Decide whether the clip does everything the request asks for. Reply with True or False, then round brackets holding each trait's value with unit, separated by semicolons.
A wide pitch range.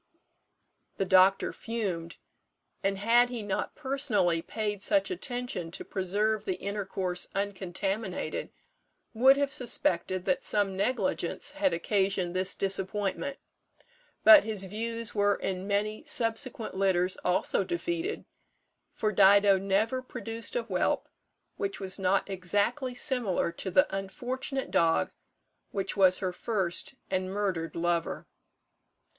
False (3.7 semitones)